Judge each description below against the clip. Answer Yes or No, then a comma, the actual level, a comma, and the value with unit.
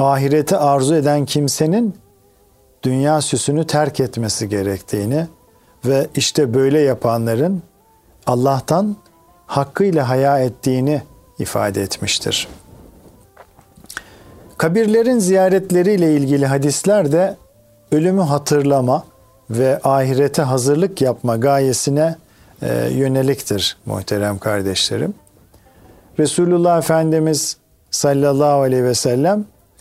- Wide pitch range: No, average, 5.0 semitones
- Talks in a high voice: No, medium, 140 Hz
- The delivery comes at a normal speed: No, slow, 80 wpm